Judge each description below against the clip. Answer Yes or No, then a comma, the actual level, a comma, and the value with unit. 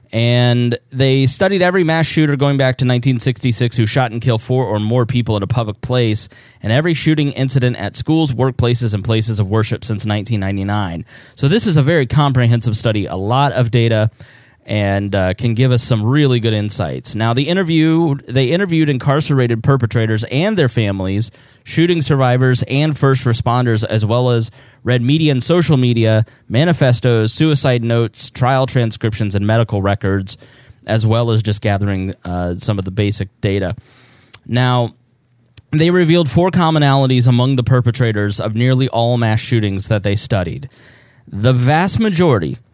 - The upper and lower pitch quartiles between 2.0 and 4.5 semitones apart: Yes, average, 3.4 semitones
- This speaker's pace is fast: No, average, 165 wpm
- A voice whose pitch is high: No, low, 120 Hz